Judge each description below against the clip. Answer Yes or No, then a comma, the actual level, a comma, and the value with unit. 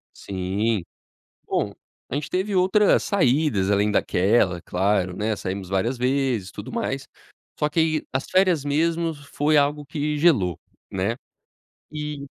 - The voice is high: No, low, 135 Hz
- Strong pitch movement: Yes, wide, 7.3 semitones